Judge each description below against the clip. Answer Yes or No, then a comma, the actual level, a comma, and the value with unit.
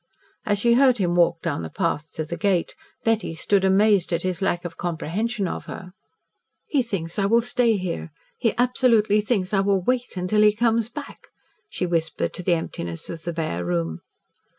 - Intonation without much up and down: No, average, 5.0 semitones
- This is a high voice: Yes, high, 195 Hz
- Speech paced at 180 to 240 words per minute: Yes, average, 190 wpm